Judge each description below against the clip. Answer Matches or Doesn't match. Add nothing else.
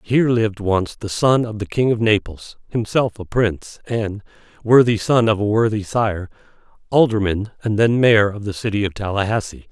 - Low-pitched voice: Matches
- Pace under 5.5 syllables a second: Matches